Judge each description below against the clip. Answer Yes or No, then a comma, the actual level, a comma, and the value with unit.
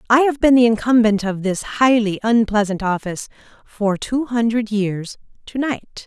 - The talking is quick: No, average, 160 wpm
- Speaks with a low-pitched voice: No, high, 225 Hz